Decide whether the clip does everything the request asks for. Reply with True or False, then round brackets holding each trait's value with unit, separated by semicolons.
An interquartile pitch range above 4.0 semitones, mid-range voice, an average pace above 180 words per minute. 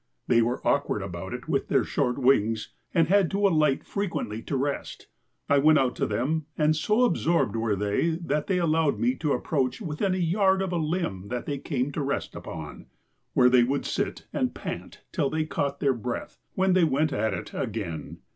True (5.2 semitones; 145 Hz; 200 wpm)